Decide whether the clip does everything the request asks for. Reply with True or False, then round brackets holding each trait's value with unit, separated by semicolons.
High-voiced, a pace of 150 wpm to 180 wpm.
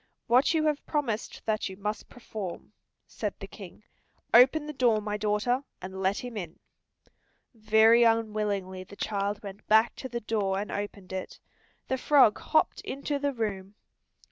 True (215 Hz; 160 wpm)